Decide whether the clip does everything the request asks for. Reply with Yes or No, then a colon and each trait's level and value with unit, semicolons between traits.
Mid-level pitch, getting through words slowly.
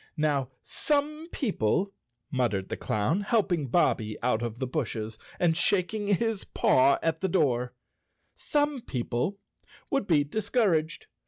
Yes: medium, 160 Hz; slow, 130 wpm